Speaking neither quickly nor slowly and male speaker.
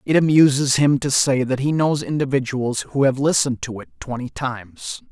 Yes: average, 190 wpm; male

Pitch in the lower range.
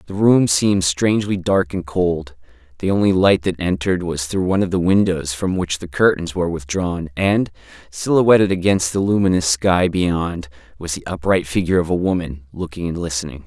Yes: very low, 90 Hz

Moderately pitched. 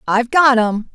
No: high, 240 Hz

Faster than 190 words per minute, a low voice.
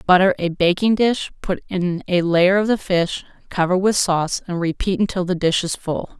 No: fast, 205 wpm; medium, 185 Hz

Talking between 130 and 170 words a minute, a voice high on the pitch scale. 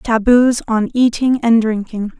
Yes: slow, 135 wpm; high, 230 Hz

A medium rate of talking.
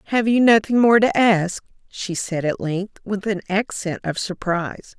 Yes: average, 180 wpm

